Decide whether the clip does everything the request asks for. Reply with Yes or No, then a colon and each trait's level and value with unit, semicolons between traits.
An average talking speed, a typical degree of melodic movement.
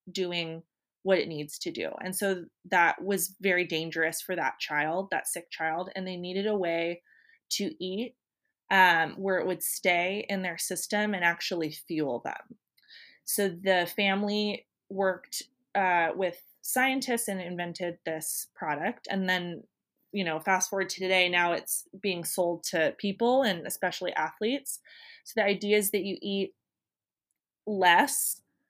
Yes: average, 155 wpm; average, 3.1 semitones